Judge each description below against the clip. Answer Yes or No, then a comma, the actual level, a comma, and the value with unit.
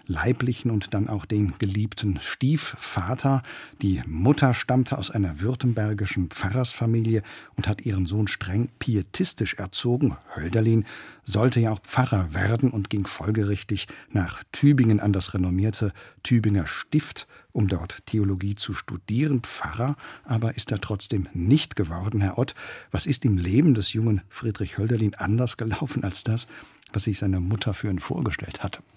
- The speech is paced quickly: No, average, 145 wpm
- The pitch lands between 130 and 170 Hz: No, low, 110 Hz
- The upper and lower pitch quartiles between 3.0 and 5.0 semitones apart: Yes, average, 3.6 semitones